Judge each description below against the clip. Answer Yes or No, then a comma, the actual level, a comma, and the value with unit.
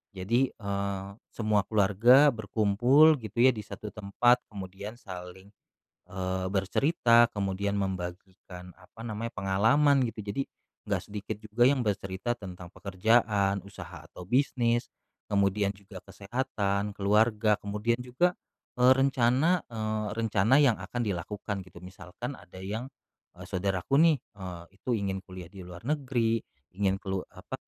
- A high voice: No, low, 105 Hz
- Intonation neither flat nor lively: Yes, average, 3.7 semitones